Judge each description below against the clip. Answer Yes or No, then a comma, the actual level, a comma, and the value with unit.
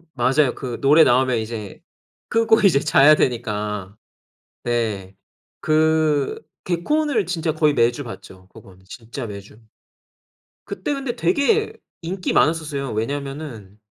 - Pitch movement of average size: No, wide, 6.1 semitones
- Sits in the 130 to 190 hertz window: Yes, medium, 140 Hz